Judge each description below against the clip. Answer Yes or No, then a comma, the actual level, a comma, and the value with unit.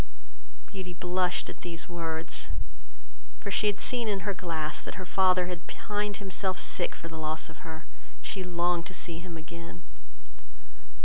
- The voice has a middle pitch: Yes, medium, 180 Hz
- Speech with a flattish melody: Yes, narrow, 2.2 semitones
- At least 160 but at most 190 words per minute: Yes, average, 165 wpm